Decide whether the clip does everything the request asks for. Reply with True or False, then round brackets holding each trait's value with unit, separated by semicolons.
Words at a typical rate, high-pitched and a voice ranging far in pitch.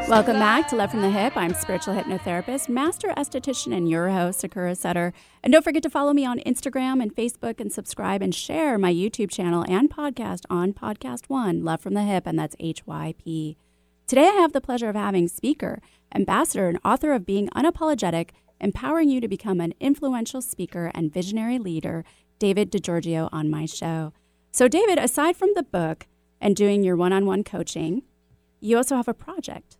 True (185 wpm; 200 Hz; 7.0 semitones)